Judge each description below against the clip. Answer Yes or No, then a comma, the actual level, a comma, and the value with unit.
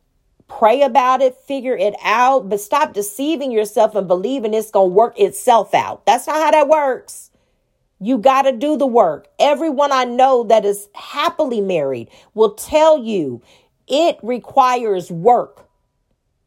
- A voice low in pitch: No, very high, 250 Hz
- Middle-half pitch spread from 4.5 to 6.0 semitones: Yes, average, 5.0 semitones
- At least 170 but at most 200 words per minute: No, average, 155 wpm